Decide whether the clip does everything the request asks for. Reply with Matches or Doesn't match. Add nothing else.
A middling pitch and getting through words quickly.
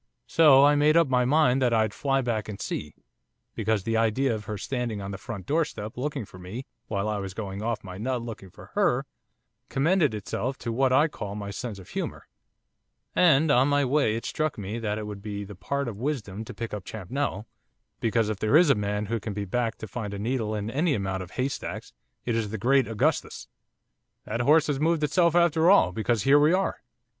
Doesn't match